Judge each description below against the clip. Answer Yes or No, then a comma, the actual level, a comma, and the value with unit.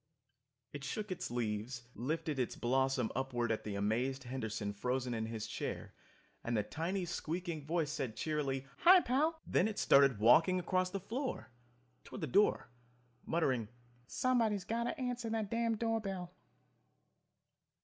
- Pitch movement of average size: No, wide, 8.7 semitones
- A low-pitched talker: No, medium, 150 Hz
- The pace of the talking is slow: No, average, 150 wpm